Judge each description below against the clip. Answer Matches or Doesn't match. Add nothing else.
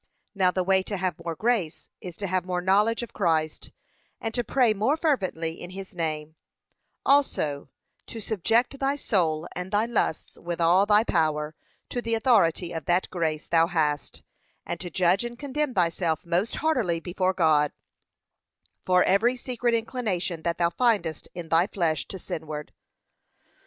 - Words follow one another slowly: Doesn't match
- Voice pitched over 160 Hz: Matches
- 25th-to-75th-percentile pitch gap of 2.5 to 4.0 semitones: Doesn't match